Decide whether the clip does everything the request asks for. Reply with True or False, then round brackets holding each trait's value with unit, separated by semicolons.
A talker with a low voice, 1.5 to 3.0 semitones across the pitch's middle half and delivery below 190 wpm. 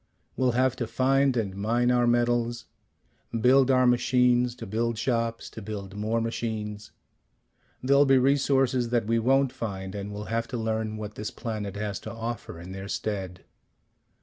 True (115 Hz; 2.7 semitones; 165 wpm)